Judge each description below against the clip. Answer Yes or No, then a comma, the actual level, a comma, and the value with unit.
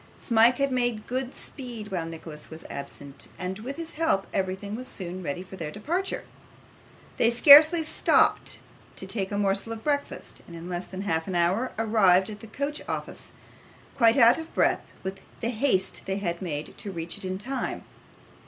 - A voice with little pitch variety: No, wide, 5.4 semitones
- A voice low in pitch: No, high, 205 Hz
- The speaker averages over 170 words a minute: Yes, average, 180 wpm